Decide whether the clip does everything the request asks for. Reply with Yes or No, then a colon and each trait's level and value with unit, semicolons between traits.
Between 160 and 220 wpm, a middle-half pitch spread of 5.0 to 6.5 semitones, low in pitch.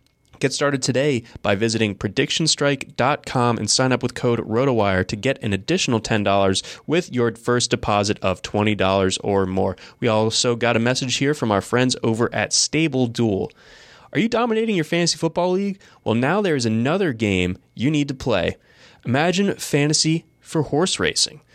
Yes: average, 165 wpm; wide, 5.4 semitones; low, 125 Hz